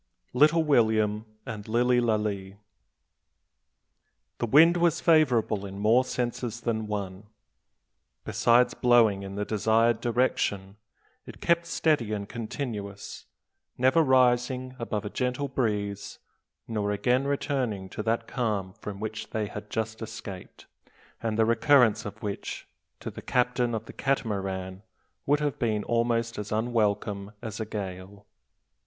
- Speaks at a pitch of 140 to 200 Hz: No, low, 110 Hz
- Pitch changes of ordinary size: Yes, average, 3.2 semitones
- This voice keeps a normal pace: No, slow, 130 wpm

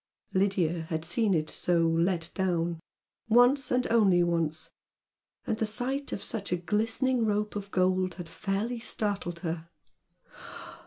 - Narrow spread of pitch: No, average, 4.5 semitones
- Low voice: No, high, 190 Hz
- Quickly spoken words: No, average, 140 wpm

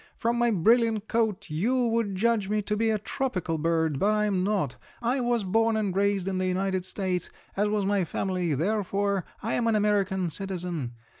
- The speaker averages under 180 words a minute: No, average, 190 wpm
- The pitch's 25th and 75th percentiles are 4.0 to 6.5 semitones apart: No, average, 3.2 semitones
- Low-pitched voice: No, high, 200 Hz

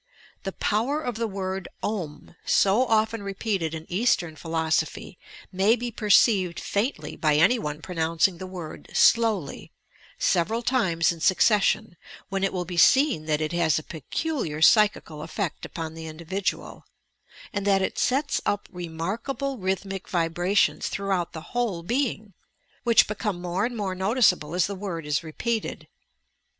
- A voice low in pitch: No, high, 190 Hz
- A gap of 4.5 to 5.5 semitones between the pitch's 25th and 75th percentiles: Yes, average, 4.8 semitones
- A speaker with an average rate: Yes, average, 150 wpm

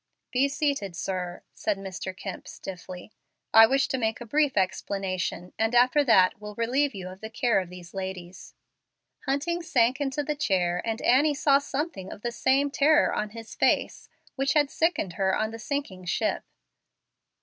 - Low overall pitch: No, high, 225 Hz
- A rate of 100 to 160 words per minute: No, average, 170 wpm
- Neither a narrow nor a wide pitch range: No, wide, 6.6 semitones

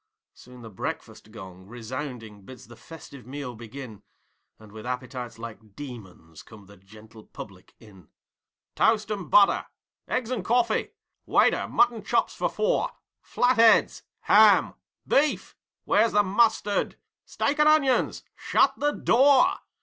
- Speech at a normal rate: No, slow, 130 wpm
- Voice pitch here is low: Yes, low, 125 Hz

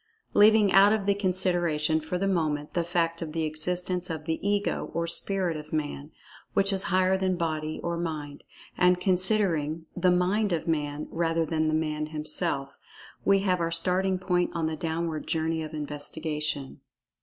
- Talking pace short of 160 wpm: No, average, 165 wpm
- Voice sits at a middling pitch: Yes, medium, 165 Hz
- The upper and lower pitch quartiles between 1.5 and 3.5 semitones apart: Yes, average, 2.9 semitones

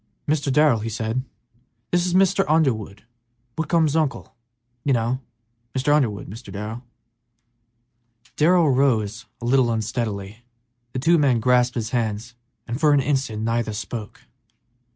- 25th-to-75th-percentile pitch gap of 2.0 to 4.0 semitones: No, average, 4.7 semitones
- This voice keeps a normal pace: No, slow, 130 wpm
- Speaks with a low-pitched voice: Yes, low, 125 Hz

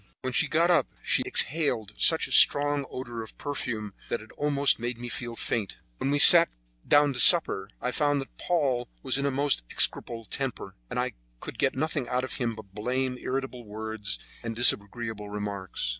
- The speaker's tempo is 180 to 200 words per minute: Yes, average, 190 wpm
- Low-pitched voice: Yes, low, 125 Hz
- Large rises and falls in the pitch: No, average, 4.3 semitones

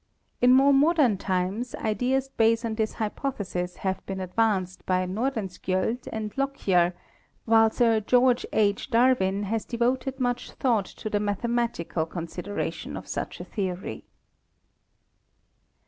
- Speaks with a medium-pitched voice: No, high, 220 Hz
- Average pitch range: Yes, average, 4.6 semitones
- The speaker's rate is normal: No, slow, 130 wpm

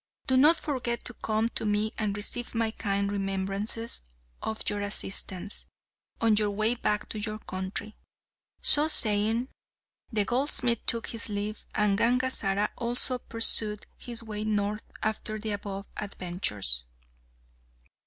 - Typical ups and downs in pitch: No, narrow, 2.2 semitones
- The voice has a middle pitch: No, high, 215 Hz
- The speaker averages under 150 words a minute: Yes, slow, 135 wpm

